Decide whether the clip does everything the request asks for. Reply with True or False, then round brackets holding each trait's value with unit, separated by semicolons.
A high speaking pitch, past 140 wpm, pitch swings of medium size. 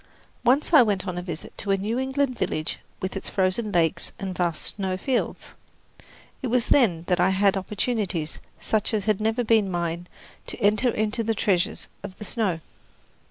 True (200 Hz; 180 wpm; 3.7 semitones)